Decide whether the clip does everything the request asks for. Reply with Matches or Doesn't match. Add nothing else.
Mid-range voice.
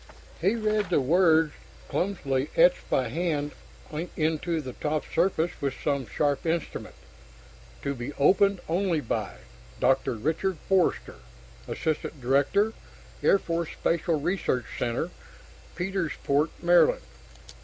Matches